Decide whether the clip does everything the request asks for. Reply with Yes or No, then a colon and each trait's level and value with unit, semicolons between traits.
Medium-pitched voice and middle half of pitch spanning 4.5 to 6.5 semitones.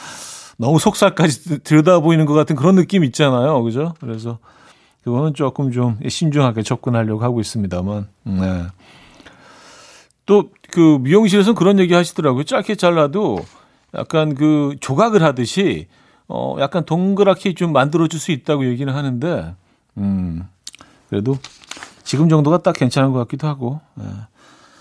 Yes: medium, 145 Hz; wide, 6.1 semitones